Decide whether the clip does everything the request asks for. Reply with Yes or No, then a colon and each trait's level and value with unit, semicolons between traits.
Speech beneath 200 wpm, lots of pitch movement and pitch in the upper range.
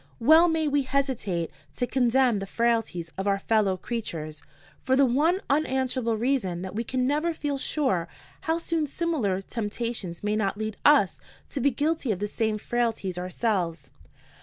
Yes: average, 160 wpm; wide, 5.9 semitones; high, 235 Hz